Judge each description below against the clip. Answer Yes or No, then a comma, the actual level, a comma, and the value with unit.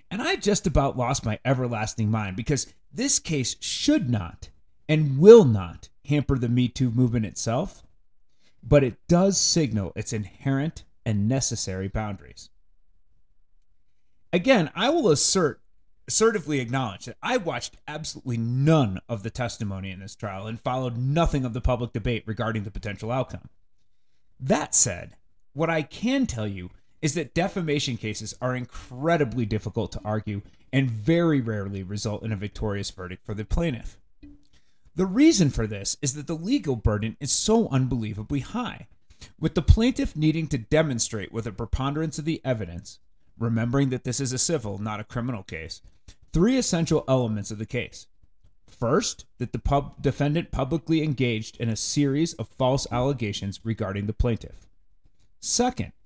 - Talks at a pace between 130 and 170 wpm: Yes, average, 155 wpm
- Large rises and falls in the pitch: Yes, wide, 5.9 semitones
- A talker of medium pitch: No, low, 120 Hz